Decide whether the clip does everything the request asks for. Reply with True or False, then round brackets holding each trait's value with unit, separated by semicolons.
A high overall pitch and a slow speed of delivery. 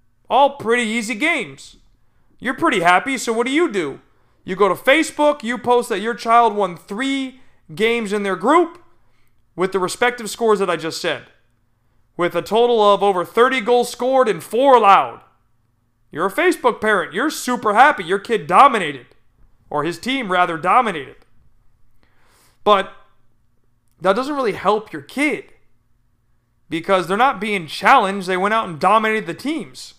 False (200 Hz; 160 wpm)